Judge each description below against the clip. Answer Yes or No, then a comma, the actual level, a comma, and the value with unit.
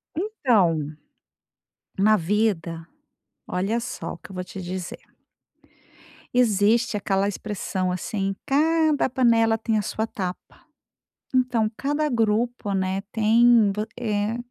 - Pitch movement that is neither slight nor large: Yes, average, 3.7 semitones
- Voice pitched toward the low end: No, high, 215 Hz